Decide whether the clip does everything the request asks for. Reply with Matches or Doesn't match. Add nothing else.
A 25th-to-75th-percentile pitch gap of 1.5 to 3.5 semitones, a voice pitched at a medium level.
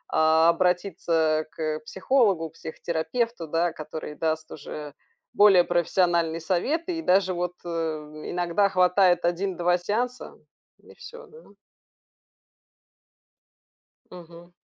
Matches